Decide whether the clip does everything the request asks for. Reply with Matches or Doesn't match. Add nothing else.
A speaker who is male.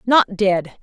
Doesn't match